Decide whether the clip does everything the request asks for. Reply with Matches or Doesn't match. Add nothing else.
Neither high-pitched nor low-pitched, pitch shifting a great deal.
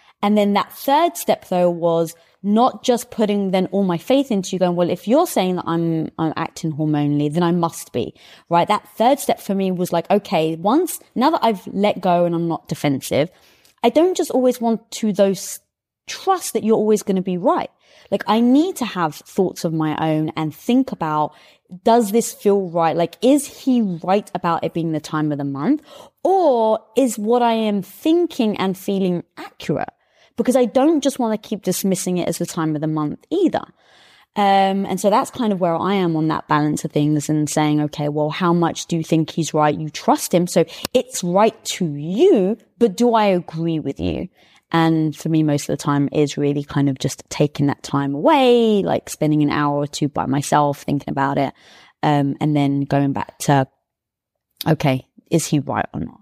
Matches